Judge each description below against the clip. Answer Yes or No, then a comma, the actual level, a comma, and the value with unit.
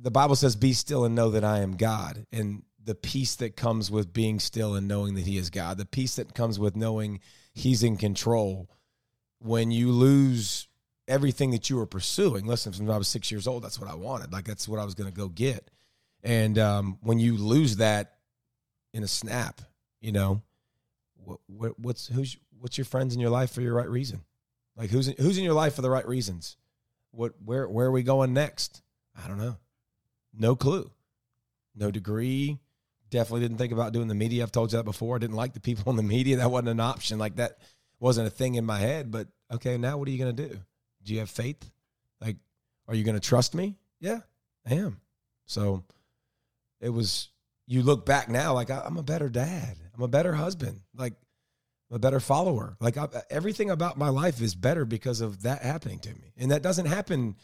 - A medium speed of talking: No, fast, 215 wpm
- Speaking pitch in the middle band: No, low, 120 Hz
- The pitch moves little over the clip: No, average, 3.0 semitones